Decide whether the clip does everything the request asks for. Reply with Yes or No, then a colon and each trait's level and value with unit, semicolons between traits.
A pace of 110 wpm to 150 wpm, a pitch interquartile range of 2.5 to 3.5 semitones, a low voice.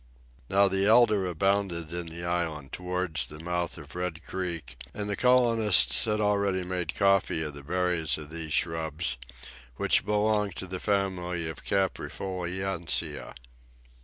Yes: average, 145 wpm; average, 3.0 semitones; very low, 90 Hz